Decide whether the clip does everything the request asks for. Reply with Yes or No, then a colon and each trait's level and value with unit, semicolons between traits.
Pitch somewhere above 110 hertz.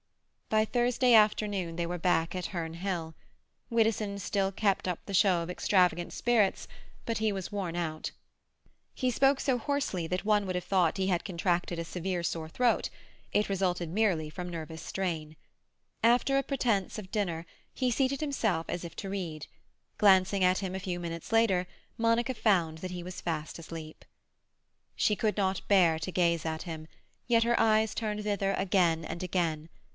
Yes: medium, 185 Hz